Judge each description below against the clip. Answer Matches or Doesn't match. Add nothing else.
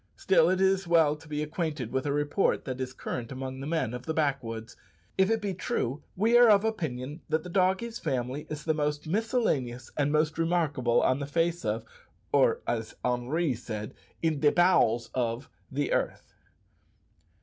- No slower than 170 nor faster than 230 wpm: Matches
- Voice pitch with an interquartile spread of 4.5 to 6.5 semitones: Matches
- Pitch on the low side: Doesn't match